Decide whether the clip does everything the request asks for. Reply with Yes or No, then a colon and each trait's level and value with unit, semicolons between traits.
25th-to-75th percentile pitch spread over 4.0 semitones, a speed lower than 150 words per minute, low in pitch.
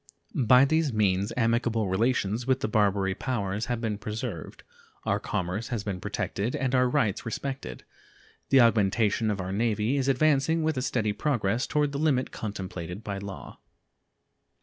No: average, 4.4 semitones; average, 155 wpm; low, 115 Hz